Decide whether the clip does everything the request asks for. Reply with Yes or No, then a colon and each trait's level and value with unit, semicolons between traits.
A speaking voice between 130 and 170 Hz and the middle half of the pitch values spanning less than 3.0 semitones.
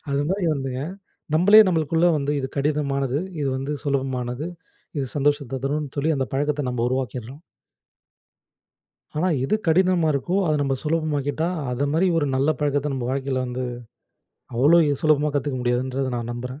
Yes: medium, 140 Hz; narrow, 2.5 semitones